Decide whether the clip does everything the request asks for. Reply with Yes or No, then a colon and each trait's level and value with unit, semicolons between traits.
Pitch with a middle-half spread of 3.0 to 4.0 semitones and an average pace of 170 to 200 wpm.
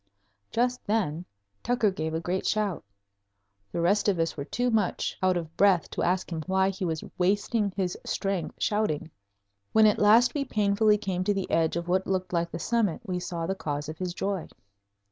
Yes: average, 3.4 semitones; average, 195 wpm